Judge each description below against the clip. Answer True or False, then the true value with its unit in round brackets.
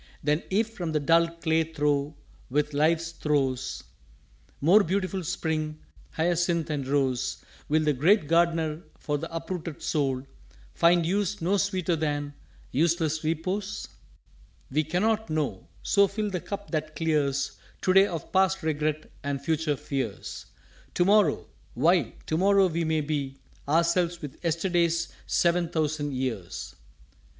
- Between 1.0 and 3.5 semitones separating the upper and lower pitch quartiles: True (3.1 semitones)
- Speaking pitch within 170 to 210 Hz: False (160 Hz)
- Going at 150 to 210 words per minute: False (140 wpm)